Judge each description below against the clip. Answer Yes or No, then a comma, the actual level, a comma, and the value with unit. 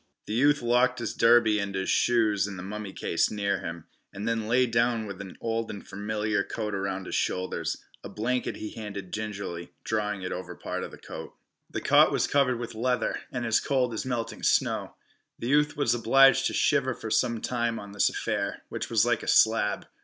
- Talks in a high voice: No, low, 110 Hz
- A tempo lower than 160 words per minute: No, fast, 205 wpm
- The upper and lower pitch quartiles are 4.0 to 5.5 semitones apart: No, average, 3.2 semitones